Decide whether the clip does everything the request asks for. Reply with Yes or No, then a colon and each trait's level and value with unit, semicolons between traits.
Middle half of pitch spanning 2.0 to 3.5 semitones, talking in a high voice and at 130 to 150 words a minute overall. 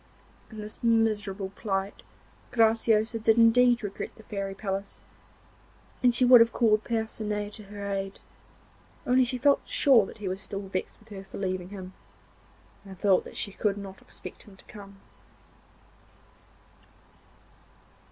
Yes: narrow, 2.6 semitones; high, 210 Hz; average, 140 wpm